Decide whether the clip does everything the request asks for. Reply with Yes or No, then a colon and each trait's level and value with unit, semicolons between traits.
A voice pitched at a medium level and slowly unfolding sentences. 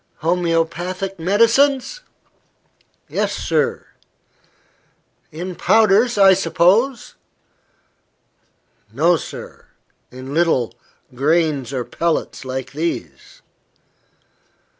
Yes: medium, 175 Hz; slow, 70 wpm